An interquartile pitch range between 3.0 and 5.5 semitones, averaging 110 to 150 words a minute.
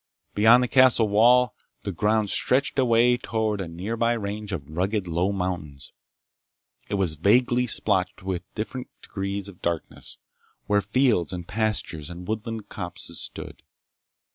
Yes: average, 4.1 semitones; average, 140 wpm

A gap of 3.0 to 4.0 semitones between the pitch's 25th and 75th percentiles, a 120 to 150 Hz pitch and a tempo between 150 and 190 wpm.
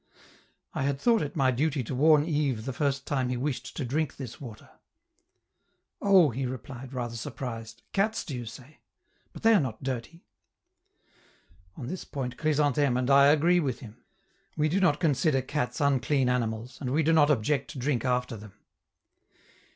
Yes: average, 3.4 semitones; low, 135 Hz; average, 175 wpm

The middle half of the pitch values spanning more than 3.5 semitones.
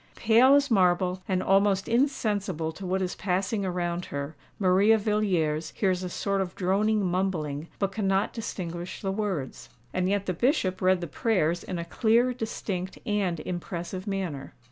No: average, 2.8 semitones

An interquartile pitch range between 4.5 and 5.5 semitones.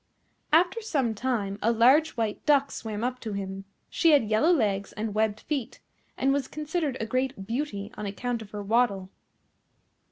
Yes: average, 5.0 semitones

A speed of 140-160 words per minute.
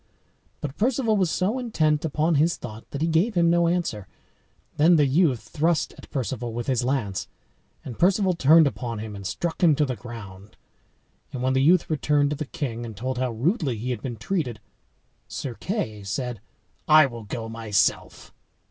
No: average, 185 wpm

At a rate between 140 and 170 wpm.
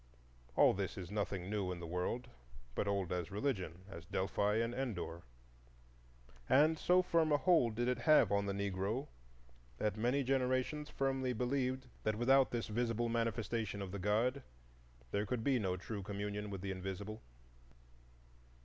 Yes: average, 160 wpm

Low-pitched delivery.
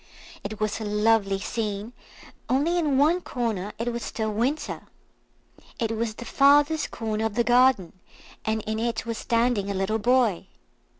No: high, 225 Hz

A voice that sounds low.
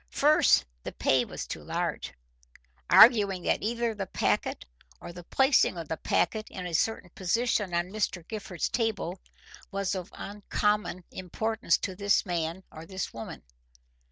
No: high, 190 Hz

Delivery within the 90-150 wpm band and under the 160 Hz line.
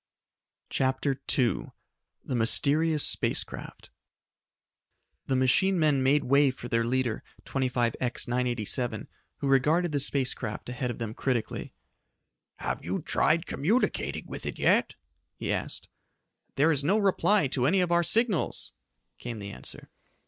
Yes: slow, 135 wpm; low, 135 Hz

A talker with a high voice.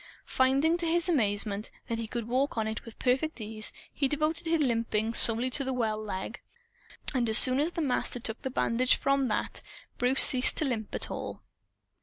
Yes: very high, 250 Hz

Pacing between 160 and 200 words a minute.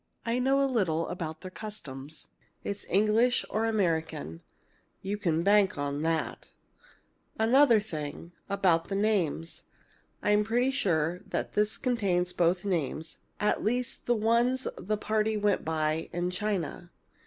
No: slow, 135 wpm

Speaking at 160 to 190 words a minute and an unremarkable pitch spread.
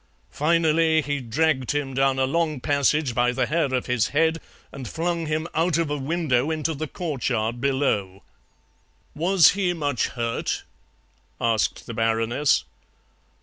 No: average, 145 wpm; average, 4.5 semitones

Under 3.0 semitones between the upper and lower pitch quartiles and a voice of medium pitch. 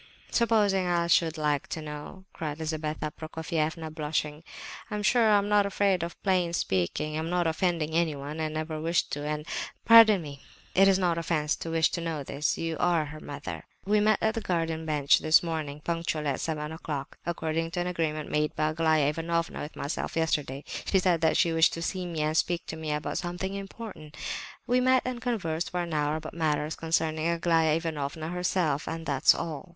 Yes: narrow, 2.5 semitones; medium, 160 Hz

